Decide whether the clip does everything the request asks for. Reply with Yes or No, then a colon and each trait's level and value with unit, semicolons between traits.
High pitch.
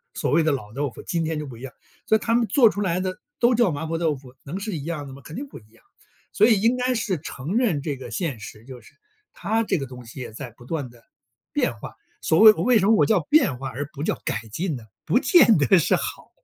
No: medium, 160 Hz